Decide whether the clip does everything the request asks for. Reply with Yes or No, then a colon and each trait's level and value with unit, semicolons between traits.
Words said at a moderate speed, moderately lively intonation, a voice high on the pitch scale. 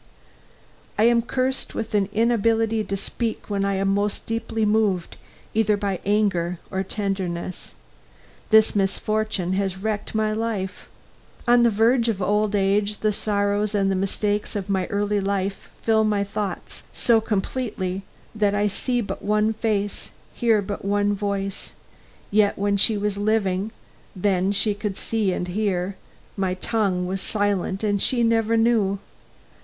No: average, 150 wpm; narrow, 1.9 semitones; high, 205 Hz